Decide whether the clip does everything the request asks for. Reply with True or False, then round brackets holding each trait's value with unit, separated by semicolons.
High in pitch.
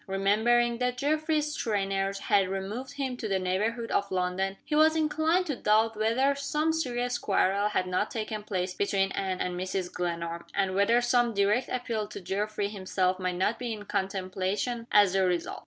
True (210 Hz)